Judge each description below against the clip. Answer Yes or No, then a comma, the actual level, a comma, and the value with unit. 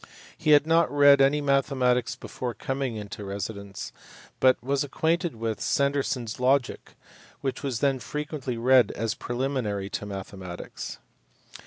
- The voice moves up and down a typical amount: Yes, average, 3.9 semitones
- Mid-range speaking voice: No, low, 130 Hz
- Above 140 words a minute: No, slow, 135 wpm